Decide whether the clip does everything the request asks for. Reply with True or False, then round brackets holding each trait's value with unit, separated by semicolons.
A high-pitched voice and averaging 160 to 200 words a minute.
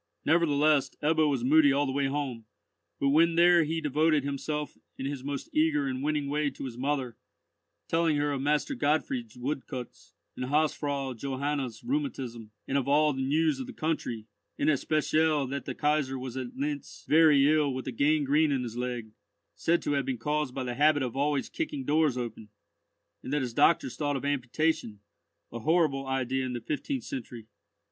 False (140 Hz; 185 wpm)